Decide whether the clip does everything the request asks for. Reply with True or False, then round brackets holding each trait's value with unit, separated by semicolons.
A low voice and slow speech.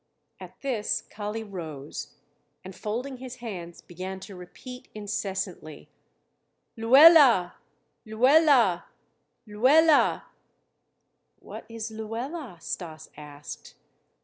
False (215 Hz; 85 wpm)